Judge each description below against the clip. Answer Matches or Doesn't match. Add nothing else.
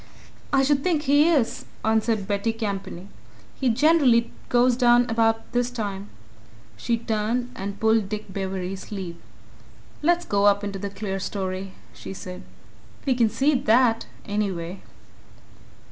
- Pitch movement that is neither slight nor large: Matches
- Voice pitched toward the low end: Doesn't match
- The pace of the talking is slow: Matches